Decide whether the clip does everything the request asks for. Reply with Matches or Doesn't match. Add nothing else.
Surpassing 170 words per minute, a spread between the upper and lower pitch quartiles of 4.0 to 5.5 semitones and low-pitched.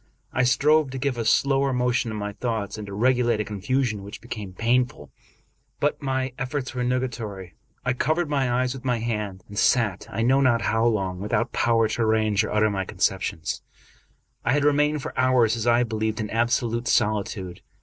Doesn't match